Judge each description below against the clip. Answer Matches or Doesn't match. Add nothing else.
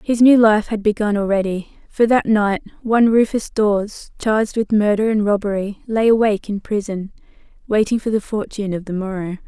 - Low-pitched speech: Doesn't match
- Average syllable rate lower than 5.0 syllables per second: Doesn't match